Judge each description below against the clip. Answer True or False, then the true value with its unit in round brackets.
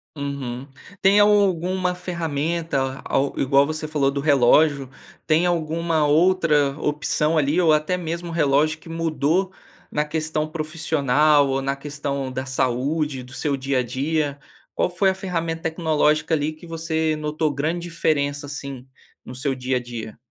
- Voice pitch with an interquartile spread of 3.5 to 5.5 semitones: False (2.8 semitones)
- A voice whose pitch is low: False (155 Hz)